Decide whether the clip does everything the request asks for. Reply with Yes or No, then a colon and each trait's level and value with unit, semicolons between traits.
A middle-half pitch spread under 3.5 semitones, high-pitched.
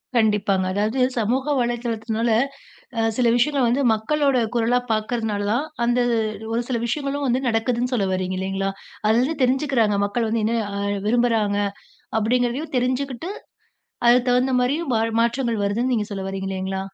Yes: average, 3.0 semitones; high, 235 Hz